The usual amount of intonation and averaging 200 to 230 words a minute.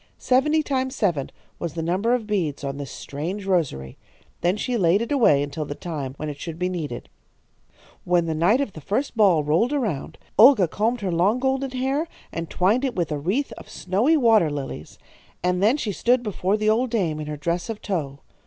No: wide, 7.3 semitones; fast, 205 wpm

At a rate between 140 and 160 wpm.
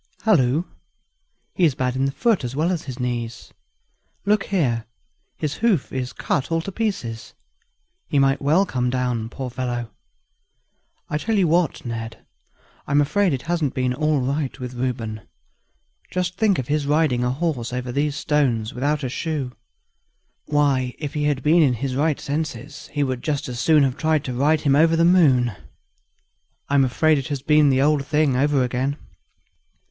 No: average, 175 wpm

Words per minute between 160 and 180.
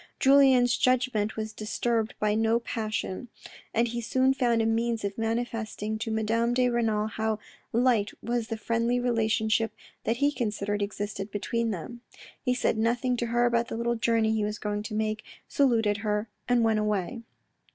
Yes: average, 170 wpm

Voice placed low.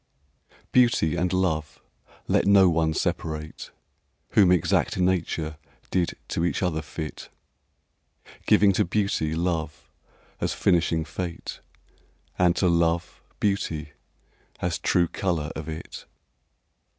Yes: very low, 85 Hz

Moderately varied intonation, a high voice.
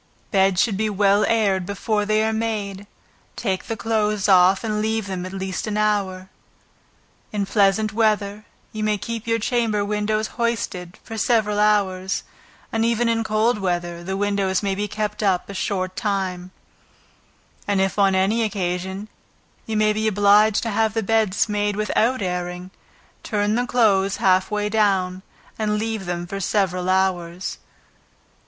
No: narrow, 2.3 semitones; high, 205 Hz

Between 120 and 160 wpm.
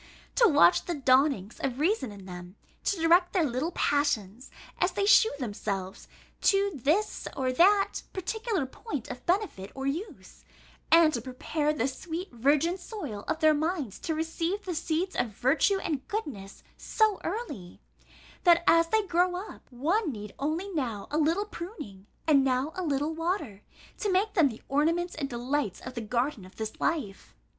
No: average, 170 wpm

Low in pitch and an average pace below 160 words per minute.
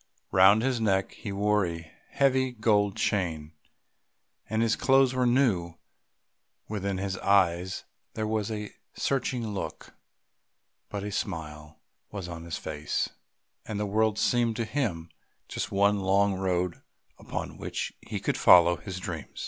Yes: low, 100 Hz; average, 140 wpm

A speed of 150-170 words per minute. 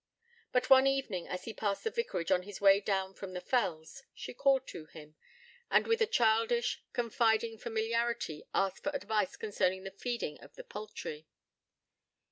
Yes: average, 165 wpm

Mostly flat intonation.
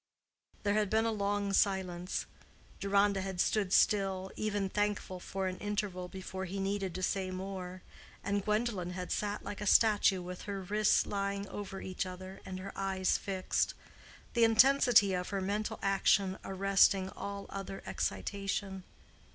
Yes: narrow, 1.5 semitones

